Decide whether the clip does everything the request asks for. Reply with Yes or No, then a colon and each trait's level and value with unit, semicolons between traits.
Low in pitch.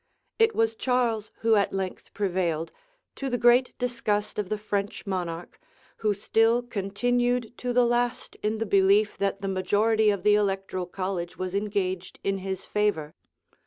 No: high, 205 Hz